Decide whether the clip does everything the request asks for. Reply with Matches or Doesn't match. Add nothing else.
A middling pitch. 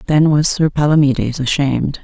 Matches